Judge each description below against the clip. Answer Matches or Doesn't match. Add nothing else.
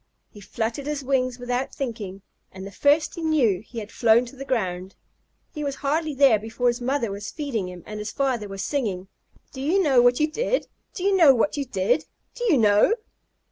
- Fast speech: Matches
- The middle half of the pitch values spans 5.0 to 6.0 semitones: Matches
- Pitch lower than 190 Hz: Doesn't match